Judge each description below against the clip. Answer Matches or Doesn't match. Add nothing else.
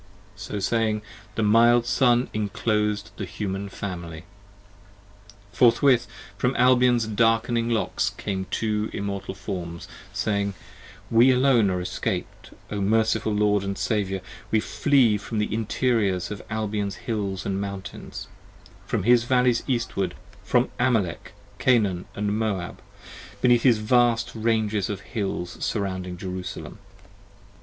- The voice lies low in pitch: Matches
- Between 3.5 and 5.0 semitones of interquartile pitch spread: Doesn't match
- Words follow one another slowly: Matches